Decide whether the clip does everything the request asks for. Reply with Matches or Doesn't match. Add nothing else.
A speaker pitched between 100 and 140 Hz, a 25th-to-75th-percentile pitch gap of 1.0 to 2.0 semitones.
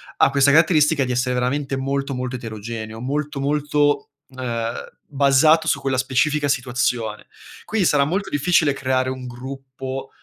Doesn't match